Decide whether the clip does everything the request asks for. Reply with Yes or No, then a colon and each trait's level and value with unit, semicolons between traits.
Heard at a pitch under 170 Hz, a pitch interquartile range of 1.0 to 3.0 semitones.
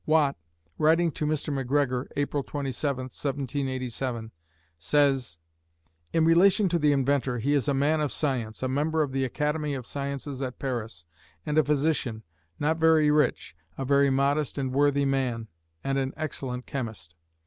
Yes: medium, 140 Hz; narrow, 2.4 semitones